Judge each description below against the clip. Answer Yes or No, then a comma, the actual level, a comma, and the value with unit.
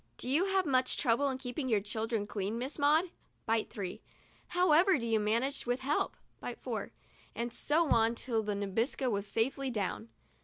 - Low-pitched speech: No, high, 245 Hz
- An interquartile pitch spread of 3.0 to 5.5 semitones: Yes, average, 4.4 semitones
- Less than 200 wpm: No, fast, 205 wpm